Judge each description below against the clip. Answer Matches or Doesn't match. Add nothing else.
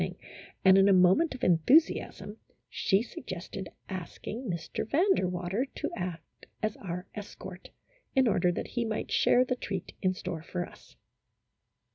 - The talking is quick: Doesn't match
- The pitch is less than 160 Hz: Doesn't match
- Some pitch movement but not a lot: Matches